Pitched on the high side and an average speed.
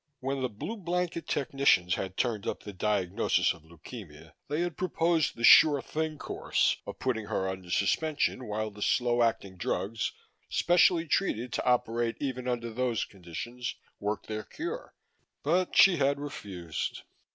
No: low, 120 Hz; average, 150 wpm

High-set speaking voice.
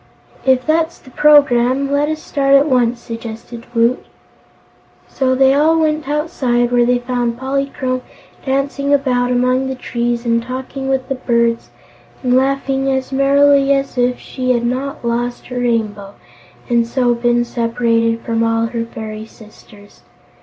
Yes: very high, 250 Hz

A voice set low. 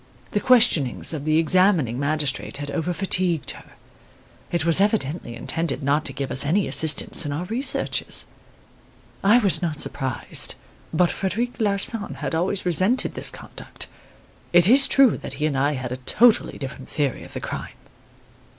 No: medium, 165 Hz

